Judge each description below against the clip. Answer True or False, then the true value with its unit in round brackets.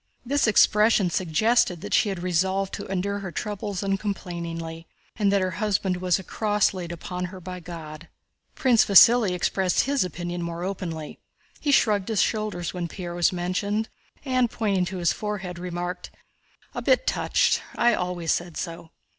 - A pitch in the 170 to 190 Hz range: True (185 Hz)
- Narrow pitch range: False (3.0 semitones)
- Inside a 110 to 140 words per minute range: False (160 wpm)